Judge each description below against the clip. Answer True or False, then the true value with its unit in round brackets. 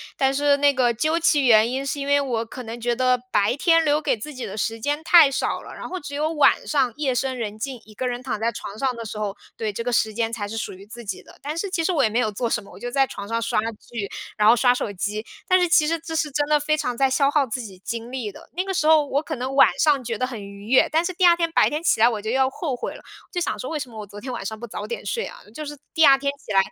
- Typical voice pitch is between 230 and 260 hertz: True (255 Hz)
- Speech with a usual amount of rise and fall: True (4.8 semitones)